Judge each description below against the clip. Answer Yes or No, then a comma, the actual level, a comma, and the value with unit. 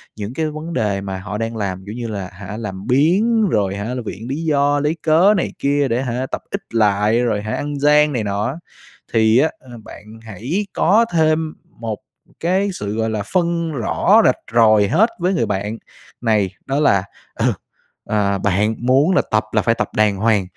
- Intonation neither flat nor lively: No, wide, 6.6 semitones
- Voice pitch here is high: No, low, 115 Hz